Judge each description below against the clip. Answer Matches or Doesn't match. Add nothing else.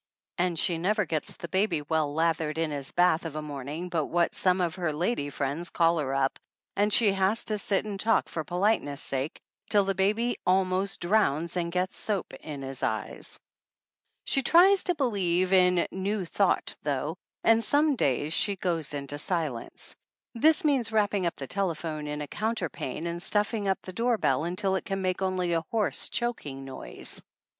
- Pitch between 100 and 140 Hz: Doesn't match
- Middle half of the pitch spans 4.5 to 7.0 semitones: Matches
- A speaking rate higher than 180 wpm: Matches